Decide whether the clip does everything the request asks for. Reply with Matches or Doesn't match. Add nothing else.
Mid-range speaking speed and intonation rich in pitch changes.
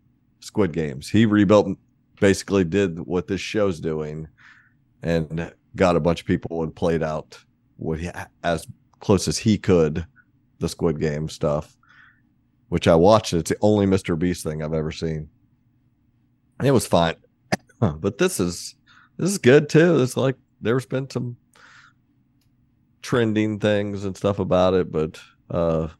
Matches